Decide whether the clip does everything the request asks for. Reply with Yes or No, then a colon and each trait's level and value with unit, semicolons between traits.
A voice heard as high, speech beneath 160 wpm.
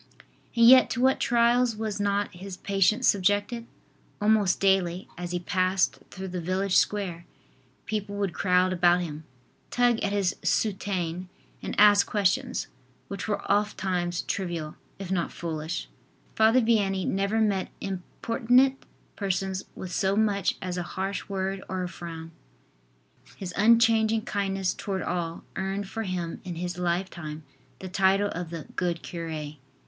Yes: high, 195 Hz; average, 145 wpm